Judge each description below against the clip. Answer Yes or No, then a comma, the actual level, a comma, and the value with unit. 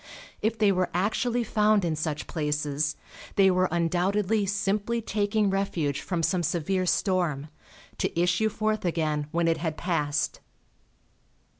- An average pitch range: Yes, average, 4.2 semitones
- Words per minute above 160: No, slow, 135 wpm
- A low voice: No, medium, 180 Hz